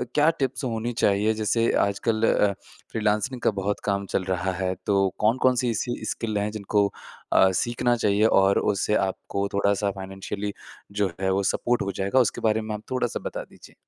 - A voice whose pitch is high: No, low, 105 Hz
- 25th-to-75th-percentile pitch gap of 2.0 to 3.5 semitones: Yes, narrow, 2.6 semitones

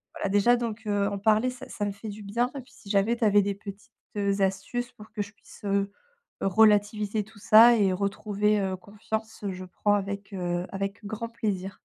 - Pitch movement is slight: Yes, narrow, 1.7 semitones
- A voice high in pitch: Yes, high, 205 Hz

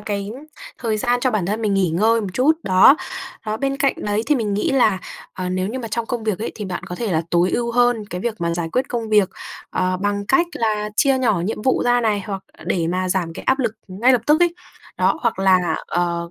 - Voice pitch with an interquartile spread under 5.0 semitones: Yes, average, 4.6 semitones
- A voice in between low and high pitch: No, high, 210 Hz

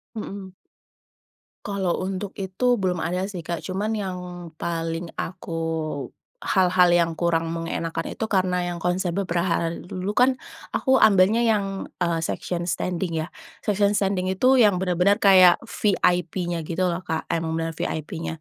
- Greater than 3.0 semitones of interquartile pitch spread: No, average, 2.7 semitones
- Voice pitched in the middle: Yes, medium, 180 Hz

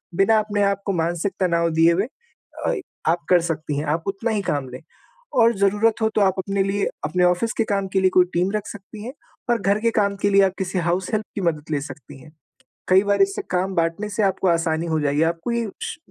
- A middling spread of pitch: Yes, average, 3.5 semitones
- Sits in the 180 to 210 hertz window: Yes, high, 190 Hz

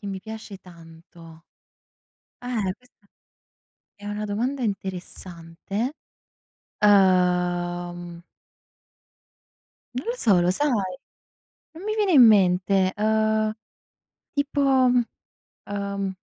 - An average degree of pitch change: Yes, average, 4.2 semitones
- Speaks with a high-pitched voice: Yes, high, 200 Hz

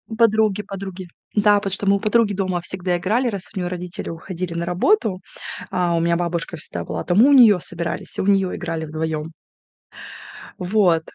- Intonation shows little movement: No, average, 3.1 semitones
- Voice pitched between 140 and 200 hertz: Yes, medium, 185 Hz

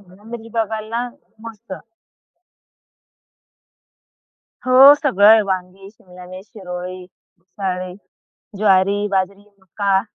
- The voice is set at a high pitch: Yes, high, 200 Hz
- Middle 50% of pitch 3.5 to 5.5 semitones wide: No, average, 3.0 semitones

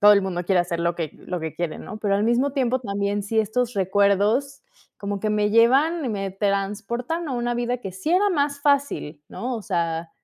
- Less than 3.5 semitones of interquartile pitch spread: No, average, 4.3 semitones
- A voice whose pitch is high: Yes, high, 210 Hz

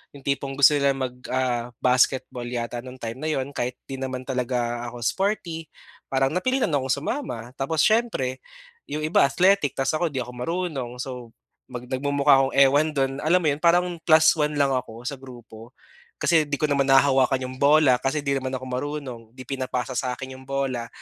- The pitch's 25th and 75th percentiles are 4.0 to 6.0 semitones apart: No, narrow, 2.6 semitones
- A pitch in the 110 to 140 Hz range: Yes, low, 135 Hz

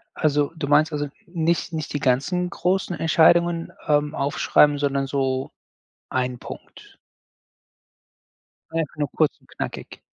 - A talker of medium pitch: Yes, medium, 150 Hz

